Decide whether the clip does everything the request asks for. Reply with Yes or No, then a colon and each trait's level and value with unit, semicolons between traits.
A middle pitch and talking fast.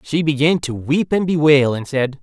Yes: medium, 145 Hz; fast, 215 wpm